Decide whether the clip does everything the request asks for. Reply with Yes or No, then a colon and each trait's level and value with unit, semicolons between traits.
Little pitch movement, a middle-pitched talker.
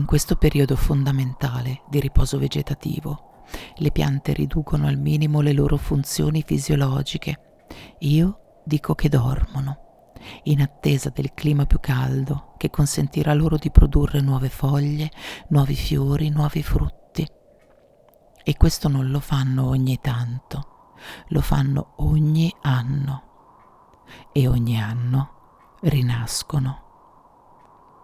Yes: narrow, 2.2 semitones; medium, 145 Hz